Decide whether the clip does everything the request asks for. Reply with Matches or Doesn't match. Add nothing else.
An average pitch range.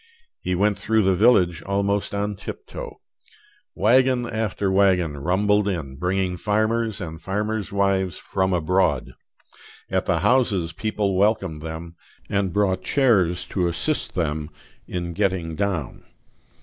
Matches